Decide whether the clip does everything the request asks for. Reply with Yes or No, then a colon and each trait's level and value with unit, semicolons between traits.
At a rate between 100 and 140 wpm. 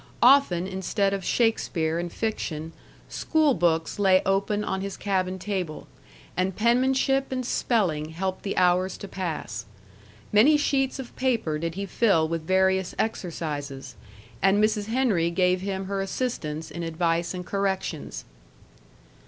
Yes: slow, 135 wpm